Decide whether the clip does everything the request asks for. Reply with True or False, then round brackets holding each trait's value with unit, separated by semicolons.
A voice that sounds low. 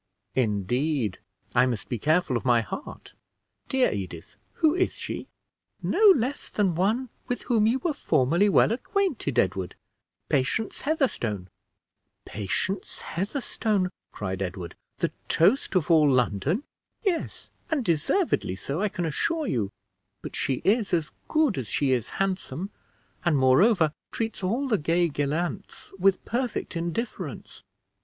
False (175 Hz)